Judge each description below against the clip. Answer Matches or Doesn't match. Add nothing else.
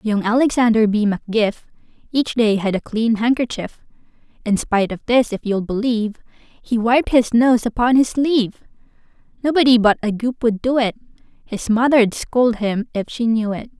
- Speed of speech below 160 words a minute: Doesn't match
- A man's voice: Doesn't match